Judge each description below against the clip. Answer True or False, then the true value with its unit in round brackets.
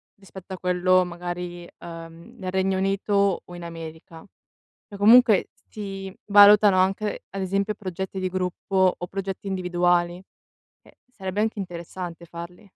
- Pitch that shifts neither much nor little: False (2.0 semitones)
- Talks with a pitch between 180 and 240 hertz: True (185 Hz)